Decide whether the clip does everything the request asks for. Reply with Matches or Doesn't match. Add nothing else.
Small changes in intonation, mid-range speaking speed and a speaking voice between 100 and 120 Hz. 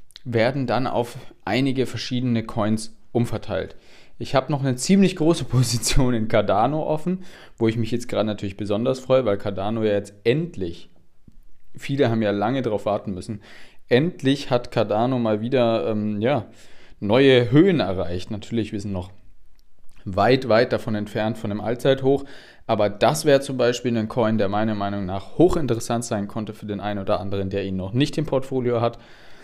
Doesn't match